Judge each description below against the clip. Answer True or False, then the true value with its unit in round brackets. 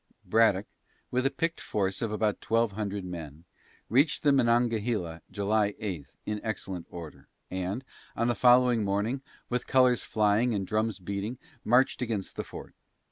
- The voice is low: True (110 Hz)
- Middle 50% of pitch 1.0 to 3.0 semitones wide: False (3.6 semitones)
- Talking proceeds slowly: False (150 wpm)